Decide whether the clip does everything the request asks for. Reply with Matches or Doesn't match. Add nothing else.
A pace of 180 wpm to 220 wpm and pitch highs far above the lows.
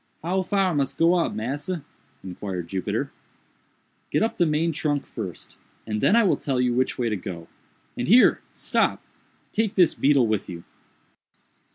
Doesn't match